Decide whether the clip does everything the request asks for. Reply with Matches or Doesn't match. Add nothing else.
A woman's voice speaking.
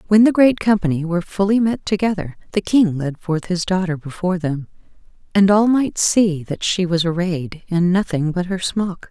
Matches